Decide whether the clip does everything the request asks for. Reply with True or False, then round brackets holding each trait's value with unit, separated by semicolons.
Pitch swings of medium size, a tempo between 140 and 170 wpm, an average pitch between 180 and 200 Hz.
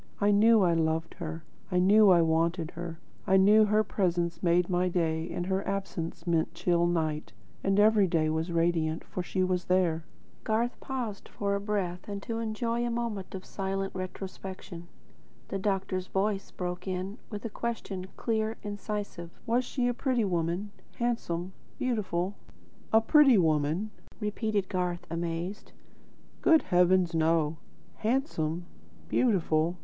True (3.6 semitones; 145 wpm; 185 Hz)